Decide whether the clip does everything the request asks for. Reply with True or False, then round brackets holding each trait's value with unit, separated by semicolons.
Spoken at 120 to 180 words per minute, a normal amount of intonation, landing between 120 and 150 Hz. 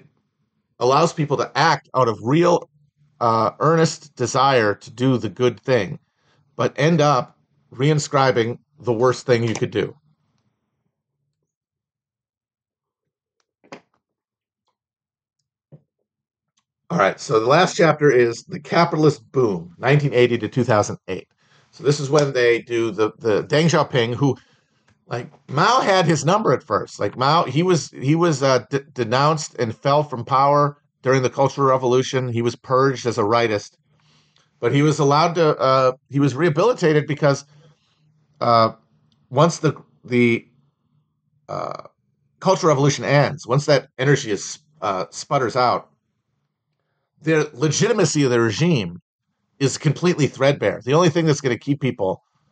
True (140 wpm; 3.6 semitones; 140 Hz)